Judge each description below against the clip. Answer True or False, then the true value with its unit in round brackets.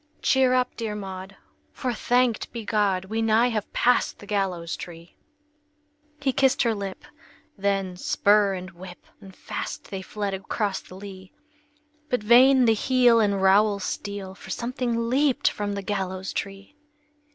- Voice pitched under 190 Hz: False (205 Hz)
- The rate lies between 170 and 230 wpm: False (150 wpm)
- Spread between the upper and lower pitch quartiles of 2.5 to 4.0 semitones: True (3.6 semitones)